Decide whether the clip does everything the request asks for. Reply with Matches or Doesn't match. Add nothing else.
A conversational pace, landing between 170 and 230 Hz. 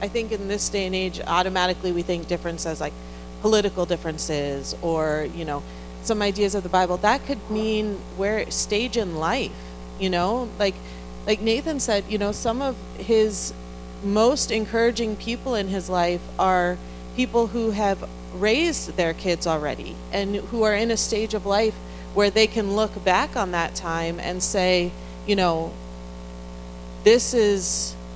Matches